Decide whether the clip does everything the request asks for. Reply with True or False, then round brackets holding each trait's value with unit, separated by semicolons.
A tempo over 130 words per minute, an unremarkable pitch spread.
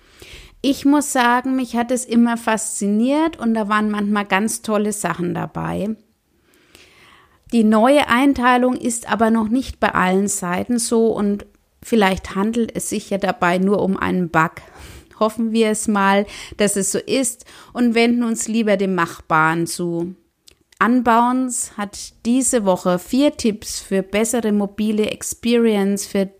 True (145 wpm; 3.4 semitones)